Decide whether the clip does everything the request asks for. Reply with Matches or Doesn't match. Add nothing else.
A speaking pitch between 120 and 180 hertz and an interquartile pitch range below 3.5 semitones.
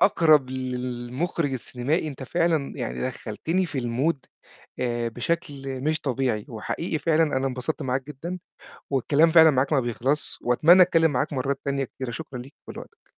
Doesn't match